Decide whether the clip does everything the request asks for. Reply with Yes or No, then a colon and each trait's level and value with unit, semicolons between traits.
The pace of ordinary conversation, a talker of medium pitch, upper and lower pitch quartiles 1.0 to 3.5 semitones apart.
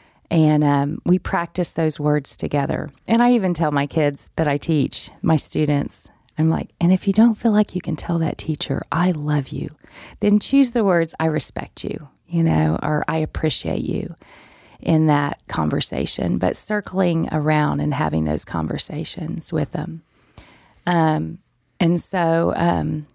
Yes: average, 165 wpm; medium, 160 Hz; average, 3.1 semitones